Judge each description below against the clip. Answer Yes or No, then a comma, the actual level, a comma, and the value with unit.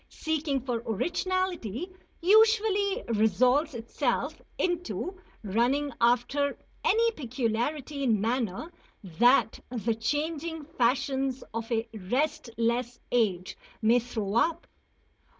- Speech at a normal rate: No, slow, 95 wpm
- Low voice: No, very high, 255 Hz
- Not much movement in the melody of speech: No, wide, 5.6 semitones